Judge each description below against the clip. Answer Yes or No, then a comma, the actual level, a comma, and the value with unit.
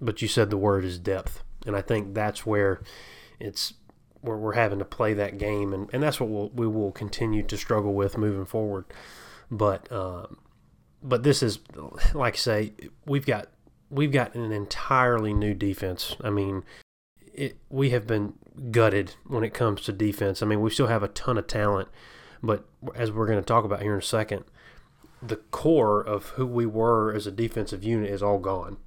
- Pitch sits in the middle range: No, low, 105 Hz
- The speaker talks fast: No, average, 195 wpm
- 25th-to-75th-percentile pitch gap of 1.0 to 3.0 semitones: Yes, narrow, 2.4 semitones